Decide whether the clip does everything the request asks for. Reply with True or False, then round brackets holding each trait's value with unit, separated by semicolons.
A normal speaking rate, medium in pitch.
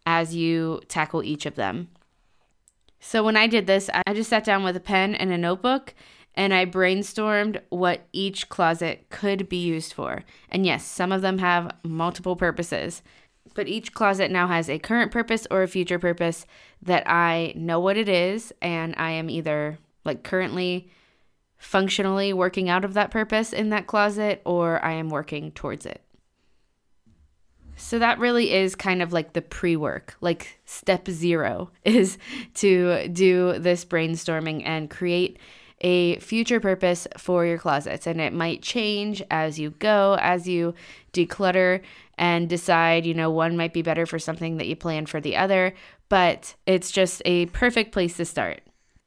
True (170 wpm; 180 Hz)